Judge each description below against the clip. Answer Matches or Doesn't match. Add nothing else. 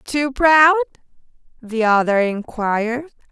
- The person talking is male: Doesn't match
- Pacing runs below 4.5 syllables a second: Matches